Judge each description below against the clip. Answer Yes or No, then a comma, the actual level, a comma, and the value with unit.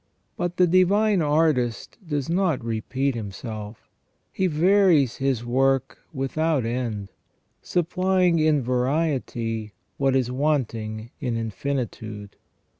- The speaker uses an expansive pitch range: Yes, wide, 5.9 semitones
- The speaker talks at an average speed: No, slow, 105 wpm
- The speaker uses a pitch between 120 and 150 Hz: Yes, low, 135 Hz